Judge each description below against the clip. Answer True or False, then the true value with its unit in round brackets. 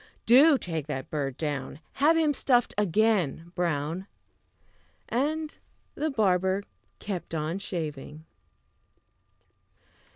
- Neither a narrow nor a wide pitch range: False (7.9 semitones)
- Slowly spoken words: True (95 wpm)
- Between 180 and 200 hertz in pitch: True (185 Hz)